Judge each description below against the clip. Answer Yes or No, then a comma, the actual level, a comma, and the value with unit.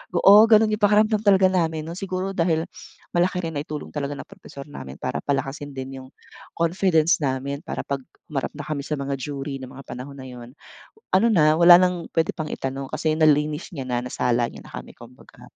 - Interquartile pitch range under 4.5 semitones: No, average, 4.8 semitones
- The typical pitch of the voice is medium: Yes, medium, 155 Hz